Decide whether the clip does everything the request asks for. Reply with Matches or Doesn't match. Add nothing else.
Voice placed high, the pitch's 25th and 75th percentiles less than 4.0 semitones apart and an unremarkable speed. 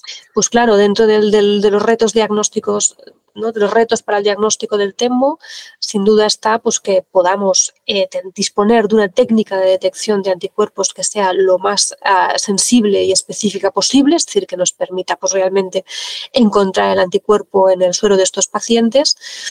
Matches